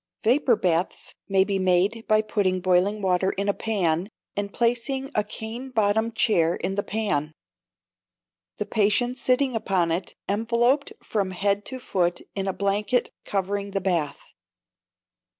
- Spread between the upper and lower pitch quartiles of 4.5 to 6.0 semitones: No, average, 3.3 semitones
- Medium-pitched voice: No, high, 200 Hz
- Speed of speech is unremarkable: Yes, average, 145 wpm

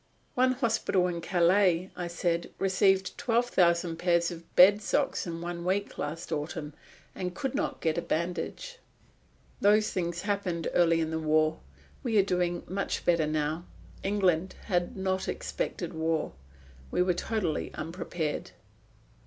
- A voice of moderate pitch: Yes, medium, 175 Hz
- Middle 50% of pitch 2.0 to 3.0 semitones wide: Yes, narrow, 2.6 semitones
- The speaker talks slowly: No, average, 145 wpm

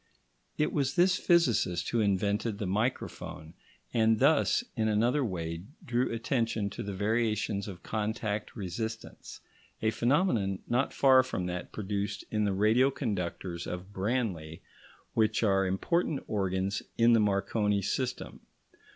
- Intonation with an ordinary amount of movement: Yes, average, 3.6 semitones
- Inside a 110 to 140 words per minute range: Yes, slow, 135 wpm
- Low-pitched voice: Yes, low, 105 Hz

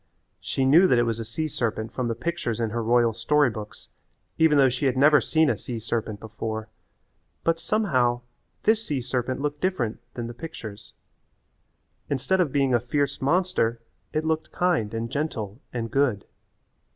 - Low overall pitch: Yes, low, 125 Hz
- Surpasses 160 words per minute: Yes, average, 175 wpm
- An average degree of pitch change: Yes, average, 4.7 semitones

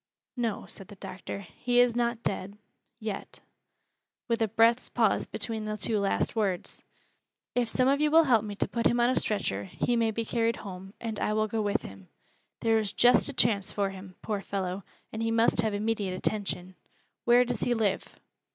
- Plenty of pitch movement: No, average, 2.9 semitones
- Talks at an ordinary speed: Yes, average, 195 wpm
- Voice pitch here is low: No, high, 220 Hz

